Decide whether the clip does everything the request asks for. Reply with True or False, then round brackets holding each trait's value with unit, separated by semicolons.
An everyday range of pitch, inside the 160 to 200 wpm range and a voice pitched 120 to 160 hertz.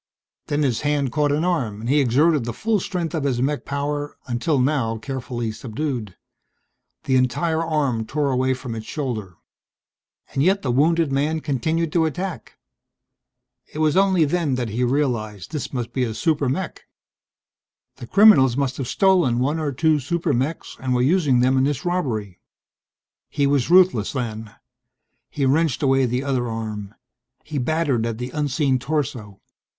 True (4.2 semitones; 165 wpm; 140 Hz)